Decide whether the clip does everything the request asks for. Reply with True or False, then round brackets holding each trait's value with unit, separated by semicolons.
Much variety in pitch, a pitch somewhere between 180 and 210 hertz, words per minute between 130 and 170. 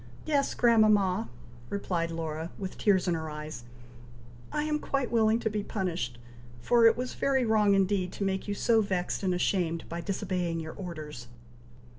False (4.7 semitones; 190 Hz; 165 wpm)